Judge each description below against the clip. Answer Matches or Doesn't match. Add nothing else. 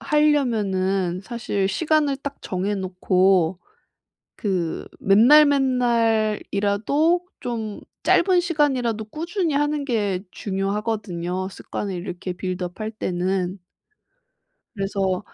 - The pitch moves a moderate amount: Doesn't match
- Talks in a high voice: Matches